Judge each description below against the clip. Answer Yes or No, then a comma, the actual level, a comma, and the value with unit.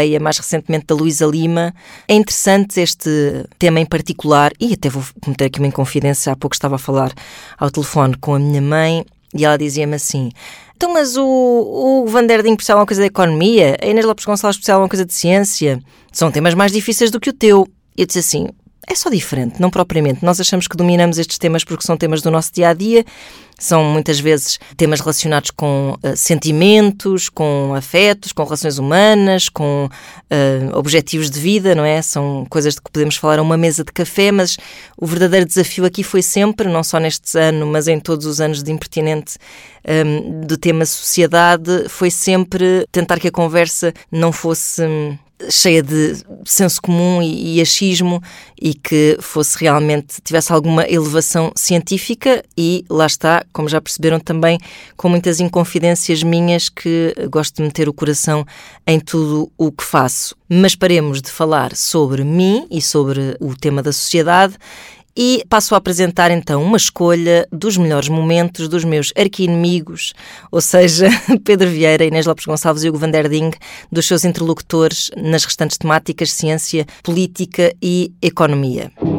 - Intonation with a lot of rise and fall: No, average, 3.0 semitones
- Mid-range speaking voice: Yes, medium, 165 Hz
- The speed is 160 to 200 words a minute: Yes, average, 170 wpm